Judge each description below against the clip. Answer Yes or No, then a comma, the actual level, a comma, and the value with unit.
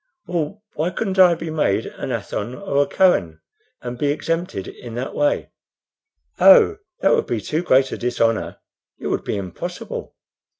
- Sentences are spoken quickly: No, average, 165 wpm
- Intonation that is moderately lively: No, wide, 6.6 semitones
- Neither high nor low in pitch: Yes, medium, 150 Hz